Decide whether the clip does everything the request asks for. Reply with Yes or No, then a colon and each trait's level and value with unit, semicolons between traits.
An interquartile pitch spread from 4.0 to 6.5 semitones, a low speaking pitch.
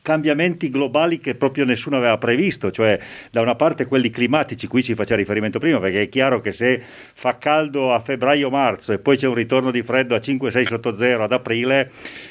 No: average, 2.9 semitones; low, 130 Hz